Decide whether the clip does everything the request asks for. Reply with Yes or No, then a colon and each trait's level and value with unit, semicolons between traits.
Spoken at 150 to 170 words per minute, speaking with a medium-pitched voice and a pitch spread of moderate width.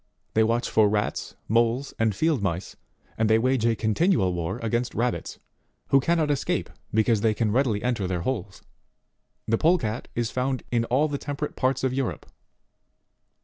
No: average, 165 wpm; low, 115 Hz; average, 3.5 semitones